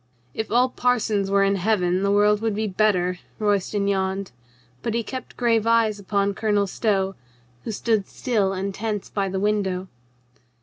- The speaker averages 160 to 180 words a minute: Yes, average, 165 wpm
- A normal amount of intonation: No, narrow, 2.2 semitones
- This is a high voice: Yes, high, 205 Hz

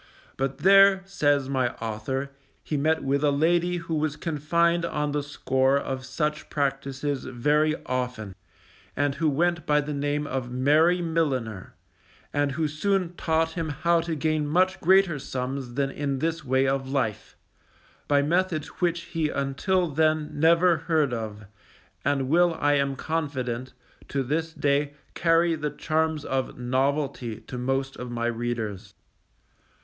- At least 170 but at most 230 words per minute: No, average, 150 wpm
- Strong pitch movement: No, average, 3.4 semitones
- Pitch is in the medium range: Yes, medium, 145 Hz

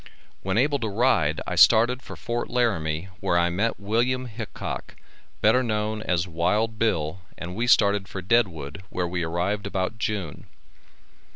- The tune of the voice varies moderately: Yes, average, 4.6 semitones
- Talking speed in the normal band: Yes, average, 155 wpm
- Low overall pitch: Yes, low, 100 Hz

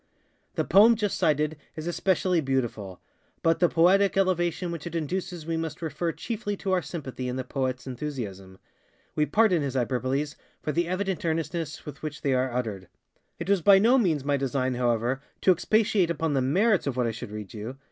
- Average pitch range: No, wide, 5.8 semitones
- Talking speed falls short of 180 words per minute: No, average, 195 wpm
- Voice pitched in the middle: Yes, medium, 155 Hz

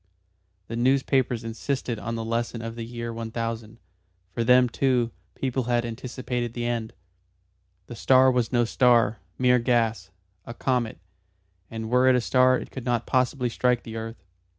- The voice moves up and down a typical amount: No, narrow, 1.7 semitones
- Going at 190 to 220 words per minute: No, average, 160 wpm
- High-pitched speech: No, low, 120 Hz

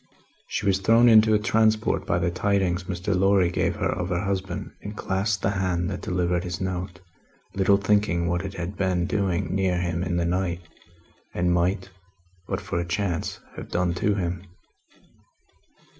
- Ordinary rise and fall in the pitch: No, narrow, 2.2 semitones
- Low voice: Yes, very low, 95 Hz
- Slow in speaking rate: No, average, 175 wpm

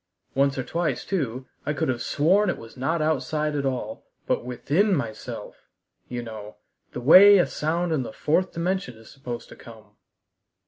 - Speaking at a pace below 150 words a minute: No, average, 175 wpm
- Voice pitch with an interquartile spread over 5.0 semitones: Yes, wide, 5.6 semitones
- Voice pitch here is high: No, medium, 140 Hz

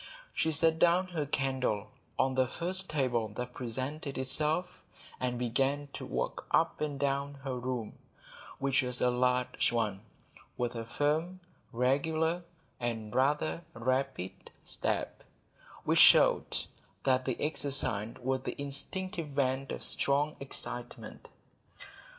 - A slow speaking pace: Yes, slow, 125 wpm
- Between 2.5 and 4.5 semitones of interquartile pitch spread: Yes, average, 3.2 semitones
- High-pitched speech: No, low, 135 Hz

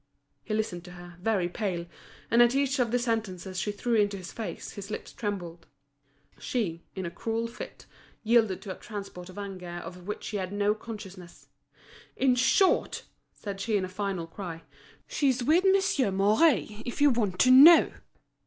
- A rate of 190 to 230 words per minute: No, average, 175 wpm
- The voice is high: Yes, high, 205 Hz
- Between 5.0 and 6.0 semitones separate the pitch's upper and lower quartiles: No, average, 4.2 semitones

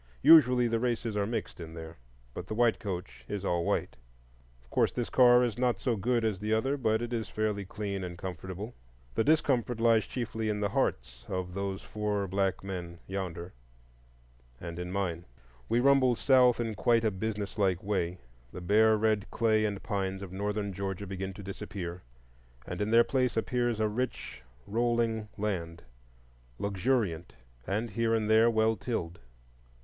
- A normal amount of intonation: Yes, average, 3.8 semitones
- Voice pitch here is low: Yes, low, 105 Hz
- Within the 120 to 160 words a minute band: No, average, 170 wpm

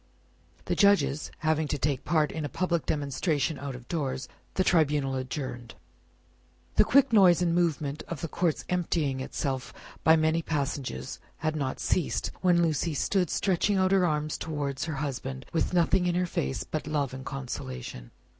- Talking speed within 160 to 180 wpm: Yes, average, 165 wpm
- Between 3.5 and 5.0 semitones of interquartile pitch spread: Yes, average, 3.9 semitones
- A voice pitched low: No, medium, 155 Hz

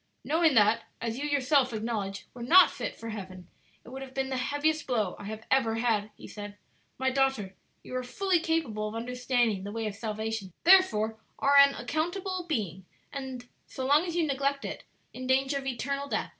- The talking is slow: No, average, 200 wpm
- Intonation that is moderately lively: Yes, average, 4.4 semitones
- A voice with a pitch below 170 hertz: No, very high, 255 Hz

